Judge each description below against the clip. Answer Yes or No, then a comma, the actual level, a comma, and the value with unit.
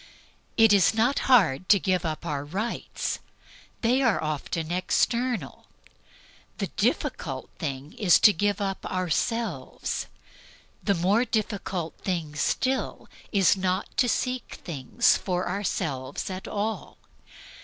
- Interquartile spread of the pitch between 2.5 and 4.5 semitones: No, average, 5.2 semitones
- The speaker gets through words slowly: Yes, slow, 120 wpm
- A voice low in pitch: No, high, 190 Hz